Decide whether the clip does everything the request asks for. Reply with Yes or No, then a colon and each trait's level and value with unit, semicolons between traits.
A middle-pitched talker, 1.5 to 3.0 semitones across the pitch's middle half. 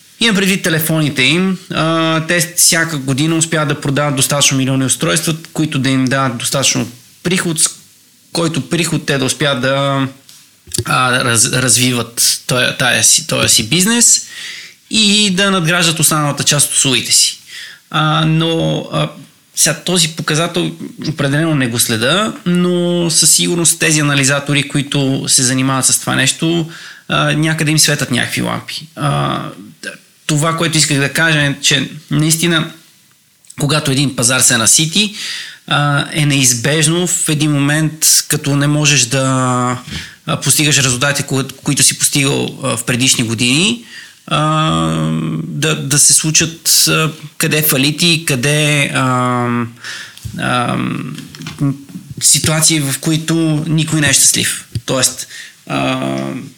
No: medium, 150 Hz; average, 3.4 semitones